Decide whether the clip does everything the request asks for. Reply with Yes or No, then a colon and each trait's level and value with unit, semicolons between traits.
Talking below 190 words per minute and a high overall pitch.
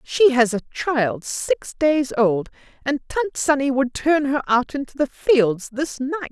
Yes: average, 180 wpm; very high, 270 Hz